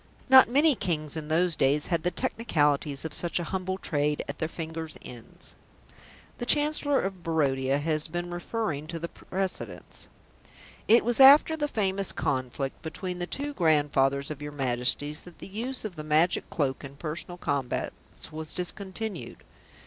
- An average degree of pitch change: Yes, average, 4.7 semitones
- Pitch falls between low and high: Yes, medium, 165 Hz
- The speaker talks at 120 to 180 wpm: Yes, average, 160 wpm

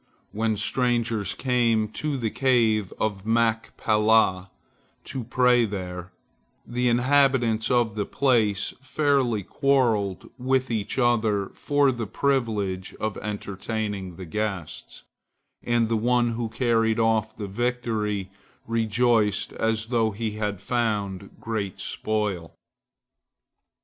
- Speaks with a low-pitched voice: Yes, low, 110 Hz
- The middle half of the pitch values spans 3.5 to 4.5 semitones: No, average, 2.7 semitones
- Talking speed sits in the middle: No, slow, 110 wpm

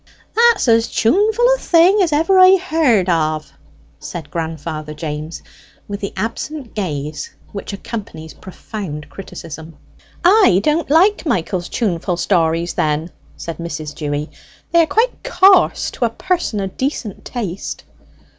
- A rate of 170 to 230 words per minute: No, slow, 135 wpm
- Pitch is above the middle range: Yes, high, 200 Hz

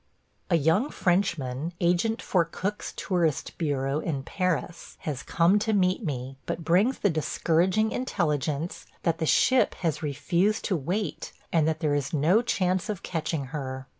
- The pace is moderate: Yes, average, 155 wpm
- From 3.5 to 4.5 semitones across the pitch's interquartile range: Yes, average, 4.0 semitones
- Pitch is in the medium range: Yes, medium, 170 Hz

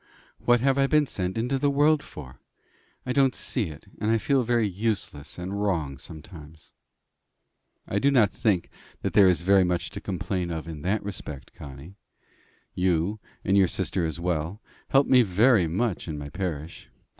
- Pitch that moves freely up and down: Yes, wide, 5.8 semitones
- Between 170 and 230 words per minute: Yes, average, 175 wpm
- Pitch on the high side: No, very low, 95 Hz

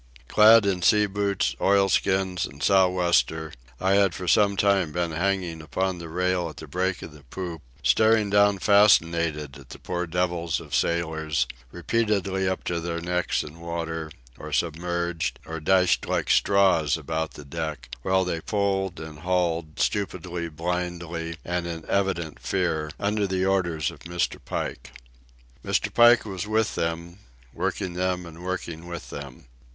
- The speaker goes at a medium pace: Yes, average, 155 wpm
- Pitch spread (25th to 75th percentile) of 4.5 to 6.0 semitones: No, average, 2.7 semitones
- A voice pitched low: Yes, very low, 90 Hz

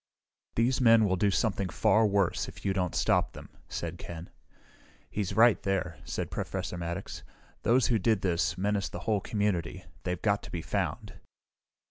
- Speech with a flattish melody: No, average, 3.5 semitones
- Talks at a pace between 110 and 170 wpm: Yes, average, 165 wpm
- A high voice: No, low, 100 Hz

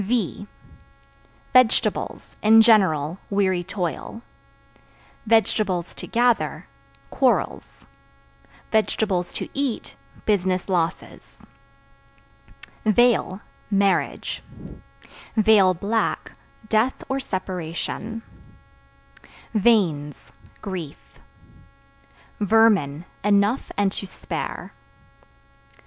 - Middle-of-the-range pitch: No, high, 200 Hz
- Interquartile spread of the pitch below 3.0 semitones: No, average, 3.6 semitones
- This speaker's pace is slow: Yes, slow, 60 wpm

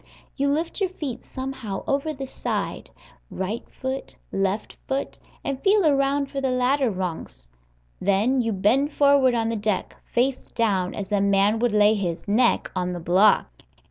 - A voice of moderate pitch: No, high, 235 Hz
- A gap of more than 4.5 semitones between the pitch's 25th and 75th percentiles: Yes, wide, 5.4 semitones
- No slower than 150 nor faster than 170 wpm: Yes, average, 165 wpm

